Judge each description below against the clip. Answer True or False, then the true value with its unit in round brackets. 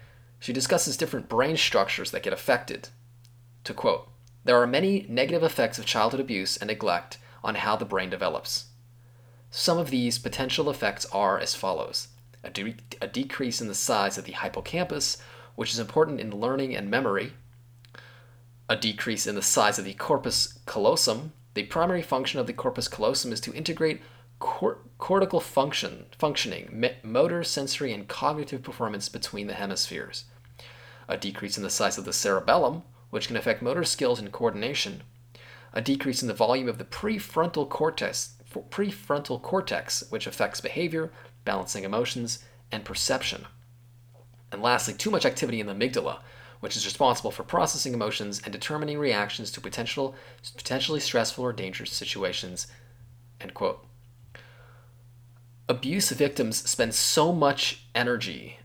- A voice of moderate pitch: False (120 Hz)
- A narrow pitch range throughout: True (2.3 semitones)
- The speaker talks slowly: False (150 wpm)